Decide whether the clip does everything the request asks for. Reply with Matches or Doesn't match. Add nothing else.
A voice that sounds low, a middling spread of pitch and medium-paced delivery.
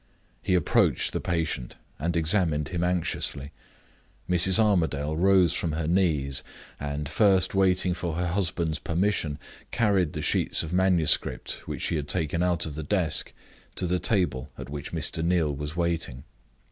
Matches